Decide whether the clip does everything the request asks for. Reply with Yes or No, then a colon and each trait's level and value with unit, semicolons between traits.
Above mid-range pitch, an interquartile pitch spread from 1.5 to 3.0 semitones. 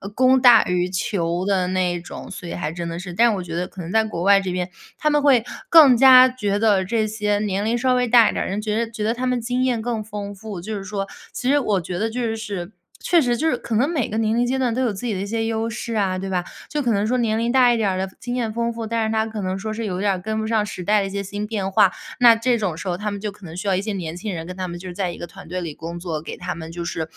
No: high, 210 Hz; average, 3.9 semitones